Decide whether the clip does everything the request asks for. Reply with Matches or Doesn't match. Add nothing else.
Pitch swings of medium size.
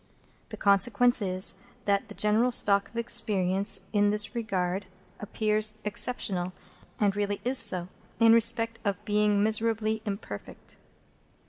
Doesn't match